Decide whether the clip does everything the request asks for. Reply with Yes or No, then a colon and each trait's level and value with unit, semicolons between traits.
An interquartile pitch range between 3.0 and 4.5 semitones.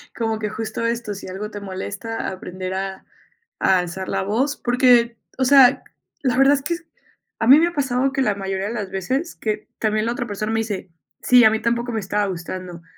Yes: average, 4.2 semitones